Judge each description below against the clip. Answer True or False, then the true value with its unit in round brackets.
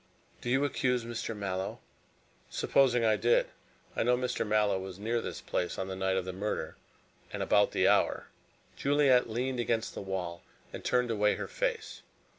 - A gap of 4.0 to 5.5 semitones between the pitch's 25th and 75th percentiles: True (4.6 semitones)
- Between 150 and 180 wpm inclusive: True (175 wpm)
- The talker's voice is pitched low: True (115 Hz)